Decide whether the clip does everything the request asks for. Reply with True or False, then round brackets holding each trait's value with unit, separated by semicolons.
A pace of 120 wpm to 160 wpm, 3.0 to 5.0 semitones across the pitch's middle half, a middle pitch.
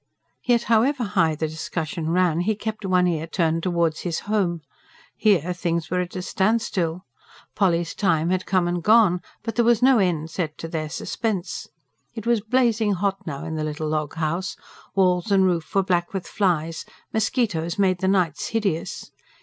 False (175 wpm; 3.9 semitones; 180 Hz)